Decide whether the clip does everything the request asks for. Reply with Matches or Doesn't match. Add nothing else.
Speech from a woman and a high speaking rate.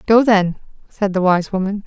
Doesn't match